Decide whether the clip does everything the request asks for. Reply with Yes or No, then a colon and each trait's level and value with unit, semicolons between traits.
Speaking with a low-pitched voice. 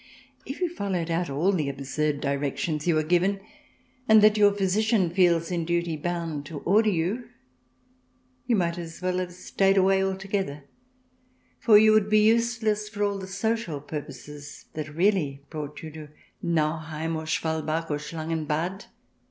No: medium, 170 Hz